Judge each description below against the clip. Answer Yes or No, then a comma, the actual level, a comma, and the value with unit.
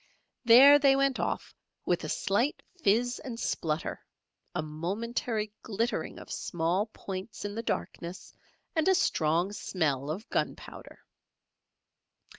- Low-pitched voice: No, high, 210 Hz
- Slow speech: Yes, slow, 120 wpm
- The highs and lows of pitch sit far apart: Yes, wide, 6.0 semitones